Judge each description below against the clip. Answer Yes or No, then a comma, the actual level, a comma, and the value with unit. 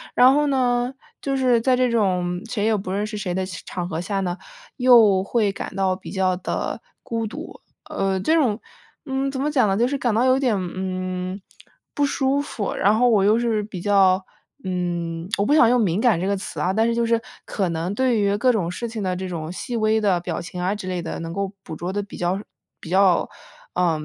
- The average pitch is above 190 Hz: Yes, high, 200 Hz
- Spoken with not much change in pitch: No, average, 4.4 semitones